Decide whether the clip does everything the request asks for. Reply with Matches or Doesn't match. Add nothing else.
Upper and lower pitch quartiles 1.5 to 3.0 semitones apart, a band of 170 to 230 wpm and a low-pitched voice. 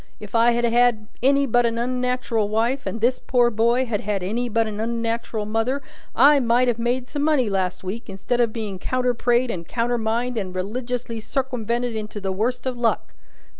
Doesn't match